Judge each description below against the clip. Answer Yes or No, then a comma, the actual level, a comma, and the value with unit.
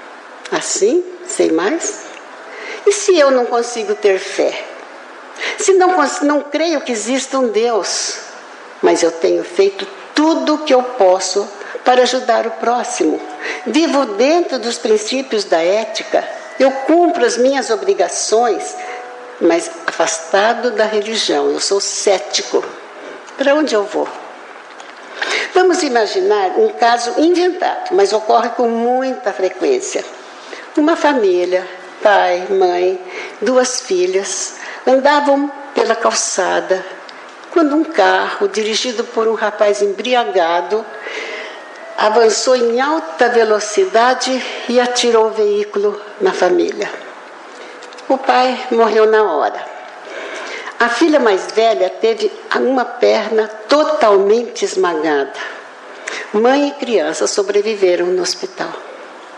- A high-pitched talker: Yes, high, 240 Hz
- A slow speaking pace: Yes, slow, 110 wpm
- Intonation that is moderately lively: No, wide, 7.1 semitones